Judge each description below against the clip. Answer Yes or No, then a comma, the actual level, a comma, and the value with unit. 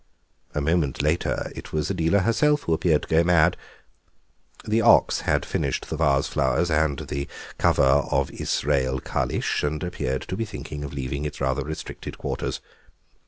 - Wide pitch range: No, average, 3.7 semitones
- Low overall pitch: Yes, very low, 75 Hz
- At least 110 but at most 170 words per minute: Yes, average, 165 wpm